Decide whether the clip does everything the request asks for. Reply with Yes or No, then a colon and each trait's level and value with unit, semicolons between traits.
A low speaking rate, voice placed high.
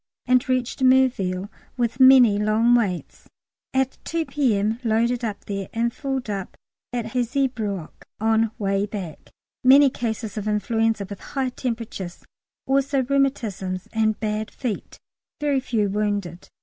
Yes: slow, 130 wpm; high, 225 Hz